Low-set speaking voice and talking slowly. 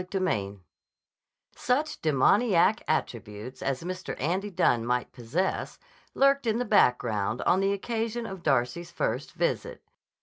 No: medium, 175 Hz; slow, 130 wpm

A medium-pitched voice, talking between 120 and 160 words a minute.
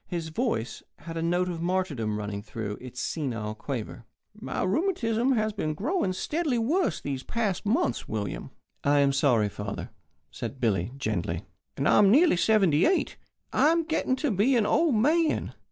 No: medium, 175 Hz; average, 170 wpm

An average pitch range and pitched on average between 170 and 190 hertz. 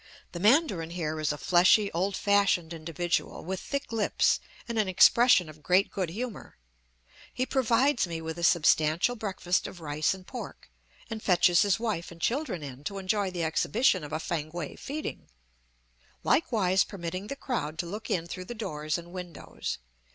Yes: average, 4.6 semitones; medium, 185 Hz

